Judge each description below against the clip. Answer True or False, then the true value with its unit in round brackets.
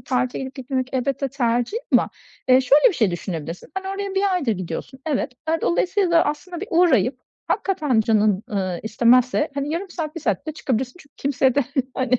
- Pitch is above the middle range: True (265 Hz)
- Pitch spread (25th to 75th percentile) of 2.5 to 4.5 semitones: False (5.1 semitones)